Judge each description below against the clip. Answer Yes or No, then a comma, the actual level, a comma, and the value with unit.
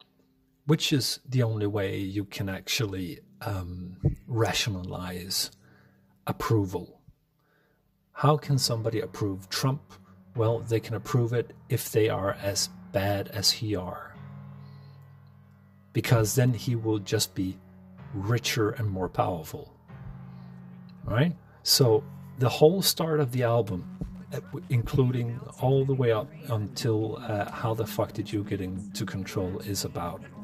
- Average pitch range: No, wide, 6.5 semitones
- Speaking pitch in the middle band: No, low, 115 Hz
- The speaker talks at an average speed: No, slow, 130 wpm